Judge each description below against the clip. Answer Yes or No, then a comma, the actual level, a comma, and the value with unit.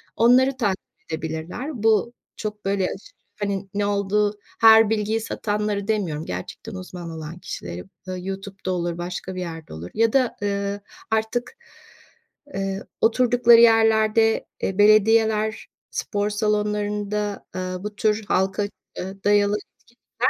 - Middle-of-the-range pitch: No, high, 205 Hz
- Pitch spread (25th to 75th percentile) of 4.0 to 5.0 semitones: No, narrow, 2.6 semitones